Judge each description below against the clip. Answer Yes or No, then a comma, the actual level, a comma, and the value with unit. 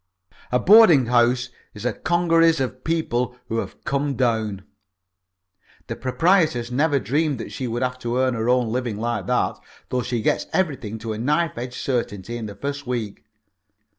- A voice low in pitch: Yes, low, 125 Hz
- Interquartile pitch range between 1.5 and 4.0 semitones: Yes, average, 3.5 semitones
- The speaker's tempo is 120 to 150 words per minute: No, average, 170 wpm